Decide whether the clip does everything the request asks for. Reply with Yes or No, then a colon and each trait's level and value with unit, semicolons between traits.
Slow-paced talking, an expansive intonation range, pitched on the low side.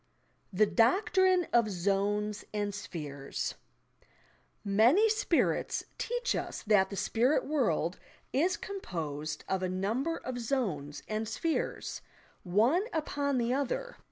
No: slow, 115 wpm; wide, 7.6 semitones; high, 220 Hz